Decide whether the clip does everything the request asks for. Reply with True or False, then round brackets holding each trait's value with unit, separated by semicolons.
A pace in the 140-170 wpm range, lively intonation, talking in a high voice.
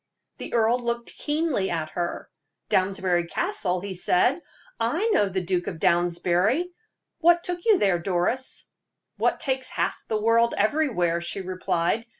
True (145 wpm; 6.7 semitones; 200 Hz)